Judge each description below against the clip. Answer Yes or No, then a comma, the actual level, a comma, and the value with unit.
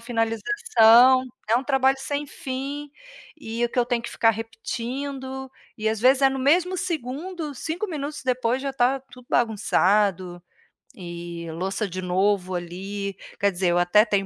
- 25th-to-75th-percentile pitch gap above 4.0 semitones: Yes, average, 5.1 semitones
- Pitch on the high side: Yes, high, 240 Hz